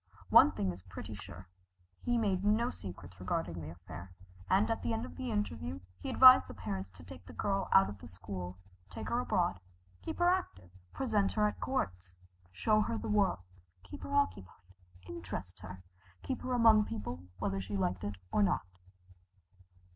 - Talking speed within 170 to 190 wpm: Yes, average, 175 wpm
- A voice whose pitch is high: No, low, 100 Hz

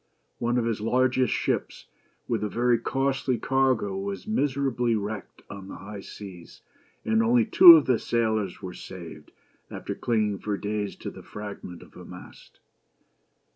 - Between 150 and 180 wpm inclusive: Yes, average, 155 wpm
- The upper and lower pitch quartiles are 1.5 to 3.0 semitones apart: No, average, 4.4 semitones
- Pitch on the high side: No, low, 110 Hz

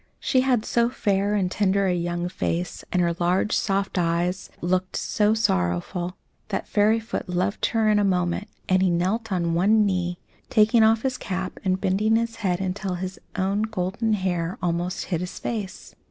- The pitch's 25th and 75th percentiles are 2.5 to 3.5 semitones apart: Yes, average, 3.1 semitones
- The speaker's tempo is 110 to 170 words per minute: No, average, 180 wpm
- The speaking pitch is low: No, high, 190 Hz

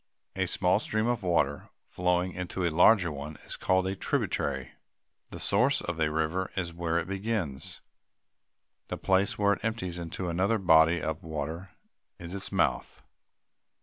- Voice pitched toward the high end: No, very low, 90 Hz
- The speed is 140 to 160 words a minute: Yes, average, 155 wpm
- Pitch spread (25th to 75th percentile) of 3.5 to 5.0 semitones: No, average, 2.9 semitones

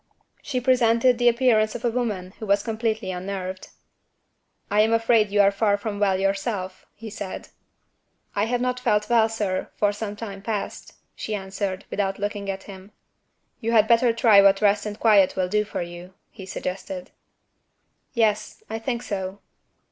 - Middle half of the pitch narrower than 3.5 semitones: Yes, narrow, 2.6 semitones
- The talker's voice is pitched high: Yes, high, 210 Hz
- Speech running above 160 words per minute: Yes, average, 170 wpm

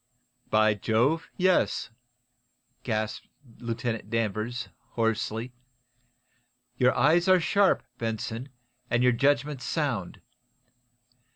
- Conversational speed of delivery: No, slow, 85 wpm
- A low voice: Yes, low, 120 Hz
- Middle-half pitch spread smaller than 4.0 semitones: No, average, 4.3 semitones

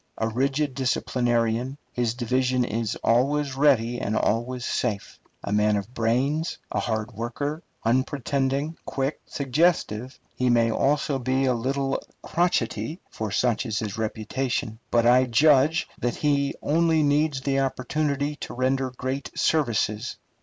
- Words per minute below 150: Yes, slow, 135 wpm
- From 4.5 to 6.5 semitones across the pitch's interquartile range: No, average, 3.4 semitones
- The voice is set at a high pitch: No, low, 130 Hz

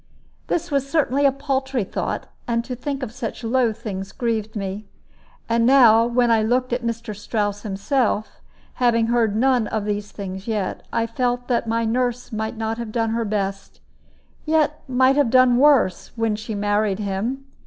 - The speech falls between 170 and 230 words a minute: Yes, average, 175 wpm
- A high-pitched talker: Yes, high, 230 Hz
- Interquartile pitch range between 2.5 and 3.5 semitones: Yes, average, 3.0 semitones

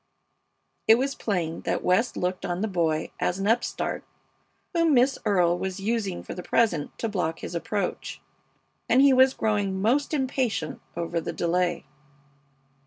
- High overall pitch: Yes, high, 195 Hz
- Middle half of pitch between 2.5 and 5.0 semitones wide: No, wide, 5.4 semitones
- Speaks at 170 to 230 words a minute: No, average, 155 wpm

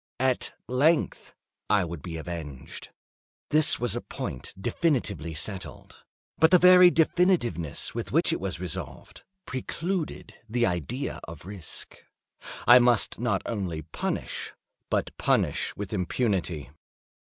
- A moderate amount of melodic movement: No, wide, 8.9 semitones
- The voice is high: No, low, 105 Hz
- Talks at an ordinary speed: No, slow, 120 wpm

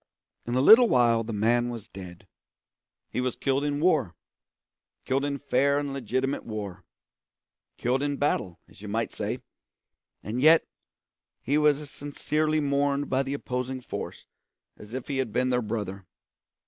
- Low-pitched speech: Yes, low, 130 Hz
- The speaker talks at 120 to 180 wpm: Yes, average, 160 wpm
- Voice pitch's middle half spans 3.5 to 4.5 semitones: Yes, average, 3.9 semitones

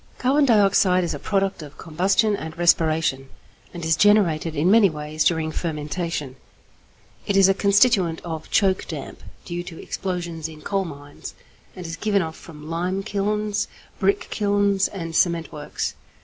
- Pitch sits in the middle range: Yes, medium, 175 Hz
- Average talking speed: Yes, average, 160 wpm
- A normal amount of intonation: Yes, average, 3.8 semitones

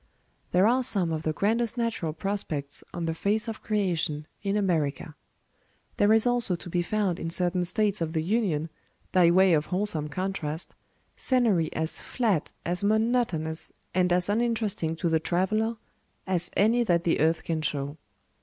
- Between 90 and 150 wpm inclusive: No, average, 165 wpm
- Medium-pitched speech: Yes, medium, 180 Hz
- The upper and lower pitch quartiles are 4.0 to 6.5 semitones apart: Yes, average, 4.7 semitones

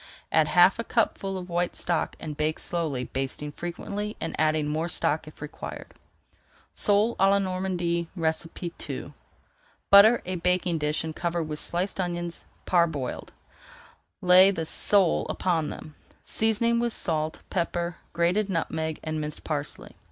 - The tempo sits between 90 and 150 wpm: Yes, average, 140 wpm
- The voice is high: No, medium, 170 Hz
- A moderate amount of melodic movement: Yes, average, 3.1 semitones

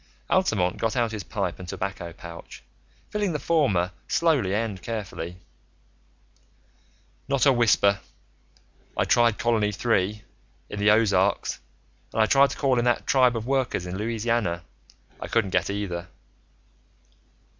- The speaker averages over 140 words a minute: No, slow, 135 wpm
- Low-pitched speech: Yes, low, 110 Hz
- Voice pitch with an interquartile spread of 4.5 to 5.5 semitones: No, average, 4.1 semitones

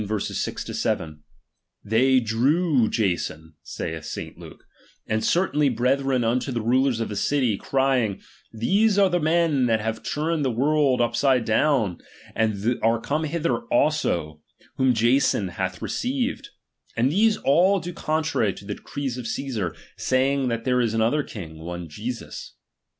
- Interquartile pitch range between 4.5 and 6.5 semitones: Yes, average, 5.1 semitones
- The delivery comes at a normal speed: Yes, average, 145 wpm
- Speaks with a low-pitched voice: Yes, low, 125 Hz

